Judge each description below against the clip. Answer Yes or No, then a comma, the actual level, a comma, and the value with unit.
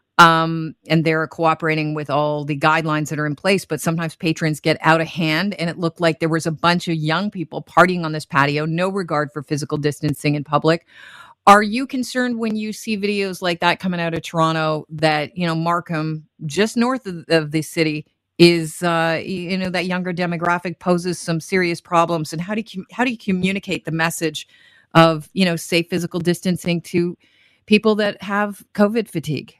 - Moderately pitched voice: Yes, medium, 165 Hz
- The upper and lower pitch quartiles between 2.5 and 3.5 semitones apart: Yes, average, 2.8 semitones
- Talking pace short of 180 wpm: No, average, 195 wpm